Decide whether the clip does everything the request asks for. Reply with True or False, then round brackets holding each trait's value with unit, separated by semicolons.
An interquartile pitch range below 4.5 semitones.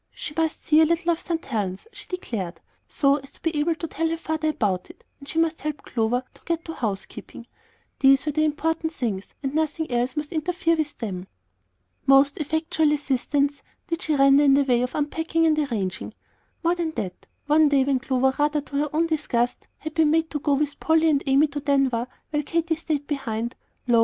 True (3.1 semitones)